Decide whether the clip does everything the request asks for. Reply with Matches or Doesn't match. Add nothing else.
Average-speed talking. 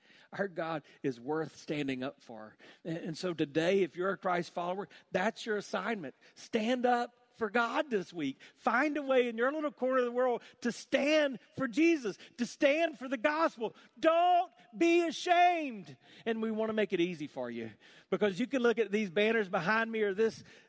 Matches